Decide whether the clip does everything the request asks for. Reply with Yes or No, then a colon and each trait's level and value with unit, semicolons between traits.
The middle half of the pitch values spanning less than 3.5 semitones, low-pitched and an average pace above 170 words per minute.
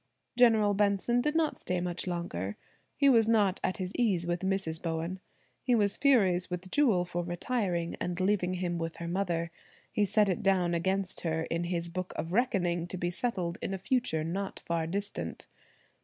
No: average, 3.1 semitones; medium, 185 Hz; average, 185 wpm